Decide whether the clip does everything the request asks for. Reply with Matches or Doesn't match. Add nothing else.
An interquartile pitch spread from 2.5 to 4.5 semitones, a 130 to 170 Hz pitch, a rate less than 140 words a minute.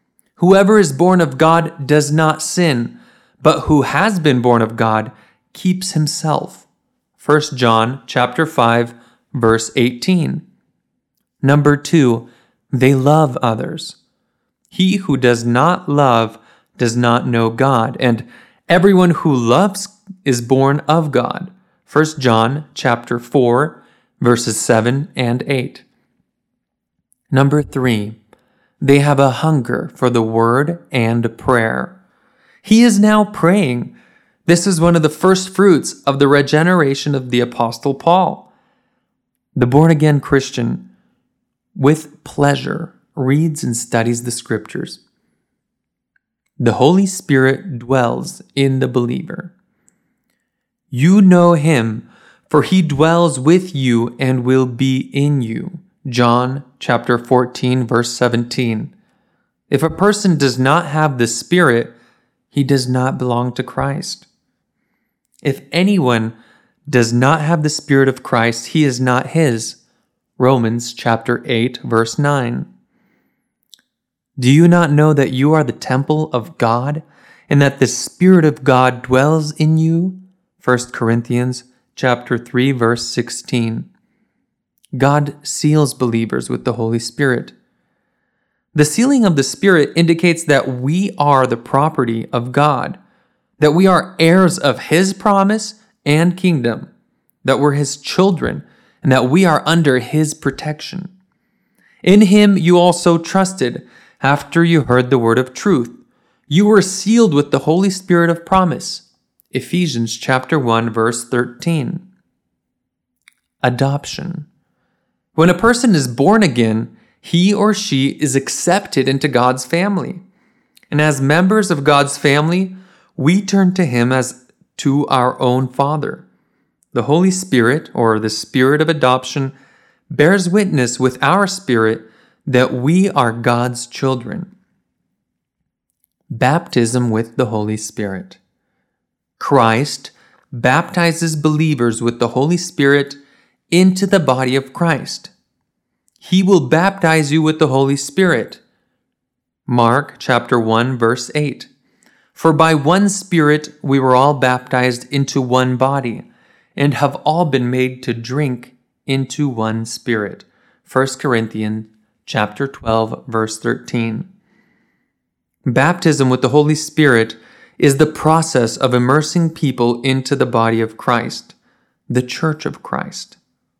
Doesn't match